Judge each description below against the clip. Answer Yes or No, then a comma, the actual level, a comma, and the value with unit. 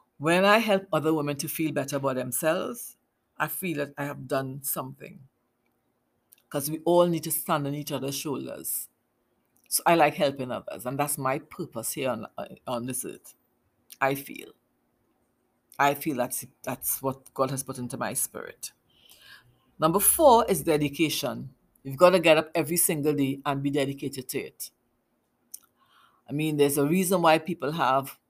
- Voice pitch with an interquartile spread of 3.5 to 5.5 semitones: No, average, 3.1 semitones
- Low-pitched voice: No, medium, 145 Hz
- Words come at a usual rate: Yes, average, 170 wpm